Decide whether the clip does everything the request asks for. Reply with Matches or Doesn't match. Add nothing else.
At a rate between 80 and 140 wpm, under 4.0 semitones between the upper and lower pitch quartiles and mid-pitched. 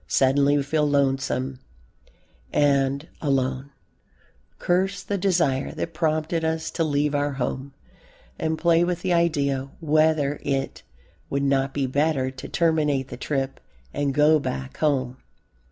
Matches